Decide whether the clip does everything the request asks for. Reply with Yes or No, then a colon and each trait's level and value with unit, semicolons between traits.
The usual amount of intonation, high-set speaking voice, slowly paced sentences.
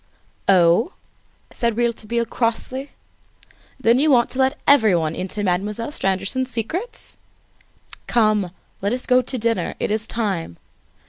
Yes: average, 4.2 semitones; high, 230 Hz; slow, 125 wpm